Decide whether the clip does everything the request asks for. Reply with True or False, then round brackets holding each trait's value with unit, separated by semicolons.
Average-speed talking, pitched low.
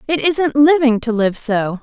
False (195 wpm; 260 Hz)